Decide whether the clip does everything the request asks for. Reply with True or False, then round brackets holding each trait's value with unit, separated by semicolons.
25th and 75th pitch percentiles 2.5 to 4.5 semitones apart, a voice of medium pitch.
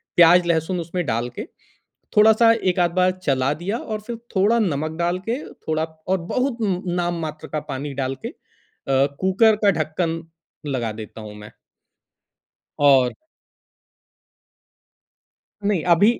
False (5.3 semitones; 170 Hz)